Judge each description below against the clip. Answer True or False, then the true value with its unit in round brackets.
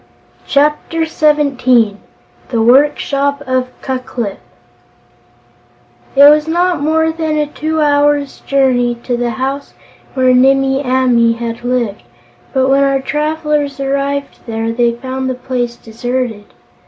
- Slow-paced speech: True (125 wpm)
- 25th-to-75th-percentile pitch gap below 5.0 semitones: True (3.0 semitones)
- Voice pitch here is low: False (270 Hz)